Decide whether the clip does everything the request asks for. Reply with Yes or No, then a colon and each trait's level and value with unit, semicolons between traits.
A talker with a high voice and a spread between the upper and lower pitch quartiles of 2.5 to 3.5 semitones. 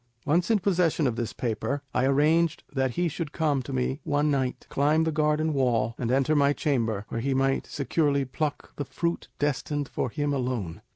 No: medium, 140 Hz; average, 3.2 semitones